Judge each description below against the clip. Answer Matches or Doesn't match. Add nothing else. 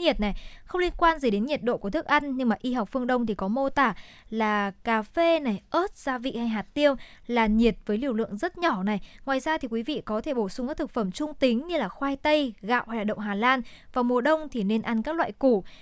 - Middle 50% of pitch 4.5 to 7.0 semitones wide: Matches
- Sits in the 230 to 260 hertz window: Matches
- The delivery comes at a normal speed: Doesn't match